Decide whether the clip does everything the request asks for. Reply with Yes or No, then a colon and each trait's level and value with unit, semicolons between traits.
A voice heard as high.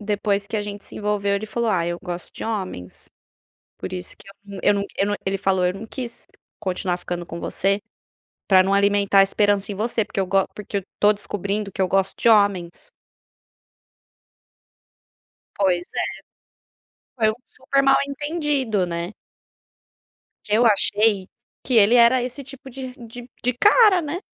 Yes: high, 205 Hz